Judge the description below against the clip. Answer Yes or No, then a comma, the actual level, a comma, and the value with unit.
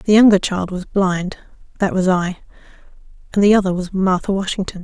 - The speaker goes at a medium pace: Yes, average, 150 wpm